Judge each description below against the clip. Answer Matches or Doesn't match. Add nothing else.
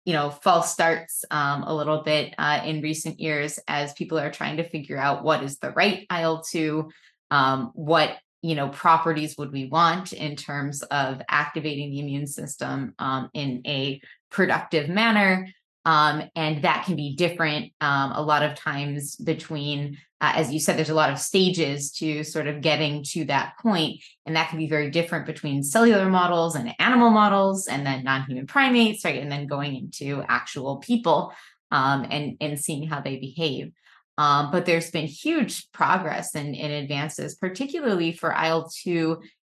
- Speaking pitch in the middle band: Matches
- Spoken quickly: Doesn't match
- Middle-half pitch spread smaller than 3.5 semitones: Matches